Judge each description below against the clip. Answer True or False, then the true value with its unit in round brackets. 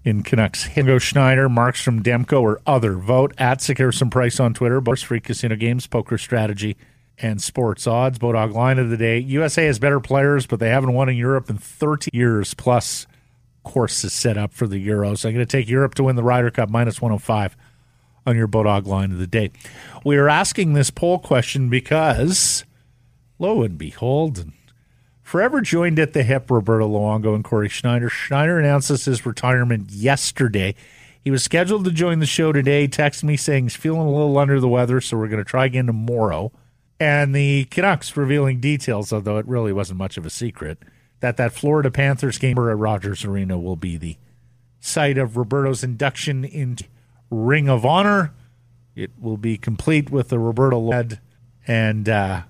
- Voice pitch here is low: True (125 Hz)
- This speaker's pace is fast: False (185 wpm)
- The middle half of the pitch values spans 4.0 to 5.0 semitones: False (3.3 semitones)